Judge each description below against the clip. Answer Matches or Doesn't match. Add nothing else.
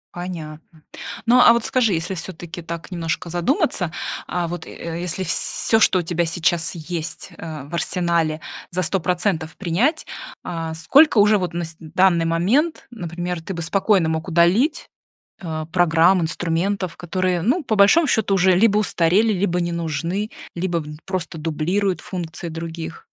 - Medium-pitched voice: Matches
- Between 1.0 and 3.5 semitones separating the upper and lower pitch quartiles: Matches